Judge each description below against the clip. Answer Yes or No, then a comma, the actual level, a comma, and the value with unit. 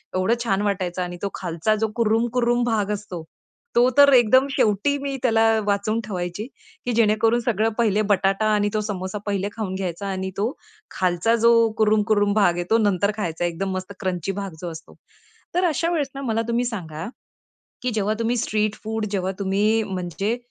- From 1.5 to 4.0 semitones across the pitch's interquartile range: Yes, average, 3.2 semitones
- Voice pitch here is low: No, high, 210 Hz